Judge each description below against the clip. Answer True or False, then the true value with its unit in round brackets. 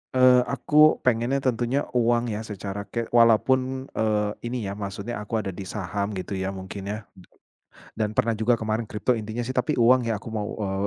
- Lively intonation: False (2.7 semitones)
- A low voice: True (110 Hz)